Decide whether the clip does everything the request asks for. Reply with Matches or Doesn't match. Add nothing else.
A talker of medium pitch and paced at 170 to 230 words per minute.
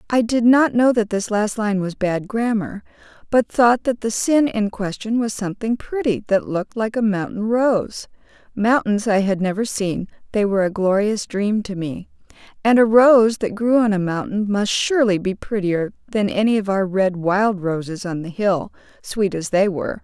Doesn't match